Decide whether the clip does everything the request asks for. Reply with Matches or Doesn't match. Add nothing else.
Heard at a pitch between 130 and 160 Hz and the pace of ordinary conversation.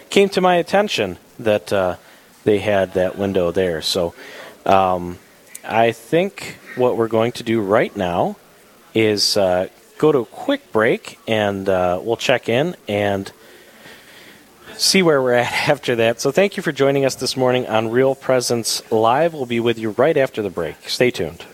Doesn't match